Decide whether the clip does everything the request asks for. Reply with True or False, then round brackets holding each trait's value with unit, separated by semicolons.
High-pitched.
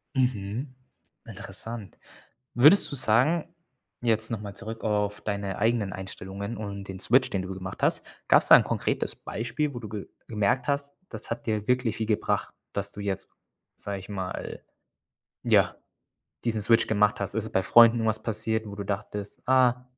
False (110 Hz)